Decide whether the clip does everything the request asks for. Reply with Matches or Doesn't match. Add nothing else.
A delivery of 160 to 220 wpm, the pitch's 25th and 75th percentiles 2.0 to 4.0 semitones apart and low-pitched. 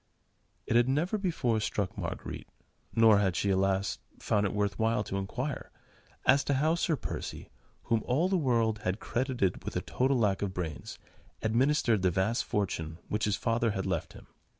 Doesn't match